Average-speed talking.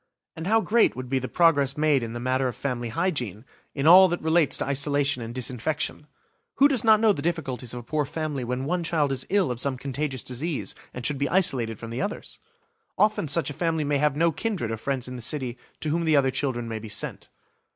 No: fast, 235 wpm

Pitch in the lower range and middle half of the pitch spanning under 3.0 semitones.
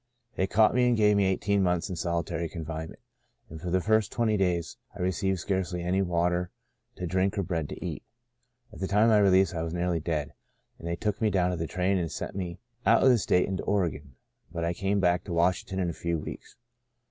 Yes: very low, 90 Hz; narrow, 2.5 semitones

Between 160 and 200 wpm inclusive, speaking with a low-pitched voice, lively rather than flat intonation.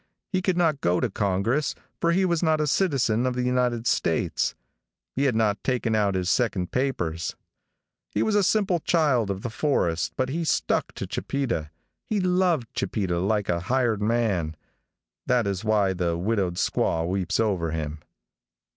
Yes: average, 170 wpm; low, 115 Hz; wide, 7.0 semitones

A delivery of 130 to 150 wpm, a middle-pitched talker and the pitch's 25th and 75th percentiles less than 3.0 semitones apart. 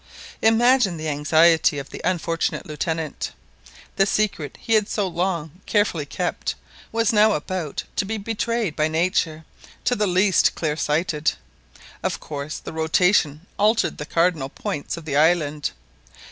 No: average, 145 wpm; medium, 170 Hz; average, 4.9 semitones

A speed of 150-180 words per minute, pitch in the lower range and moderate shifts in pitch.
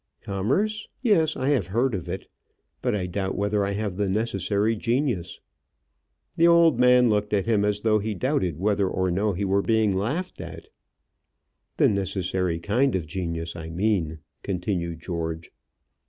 Yes: average, 160 wpm; low, 100 Hz; average, 4.0 semitones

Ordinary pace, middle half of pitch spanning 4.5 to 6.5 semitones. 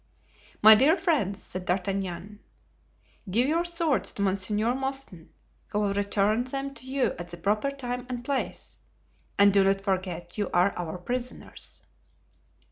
Yes: average, 145 wpm; wide, 5.4 semitones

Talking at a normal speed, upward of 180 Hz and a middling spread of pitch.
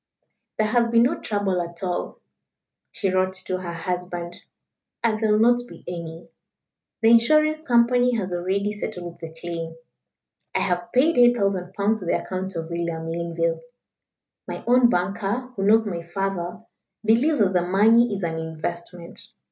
Yes: average, 155 wpm; high, 190 Hz; average, 4.6 semitones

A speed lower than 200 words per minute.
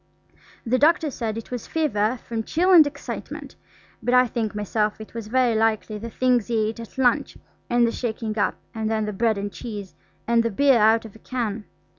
No: fast, 205 wpm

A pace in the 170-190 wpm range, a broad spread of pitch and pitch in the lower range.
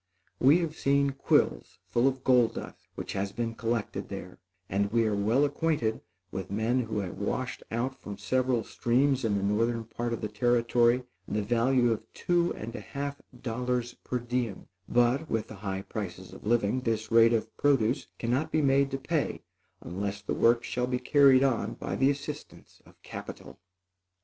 No: average, 180 wpm; average, 3.3 semitones; low, 120 Hz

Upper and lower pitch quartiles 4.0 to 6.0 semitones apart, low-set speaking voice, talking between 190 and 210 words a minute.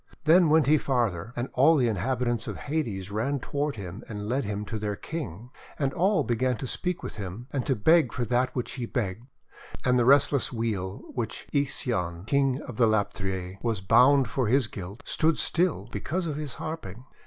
Yes: average, 5.2 semitones; low, 125 Hz; average, 200 wpm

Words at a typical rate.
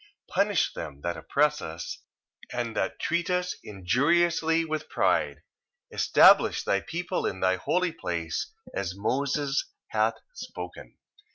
No: slow, 130 wpm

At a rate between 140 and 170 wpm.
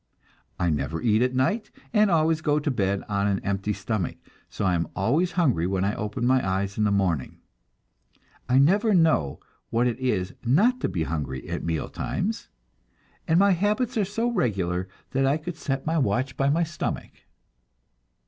No: average, 180 wpm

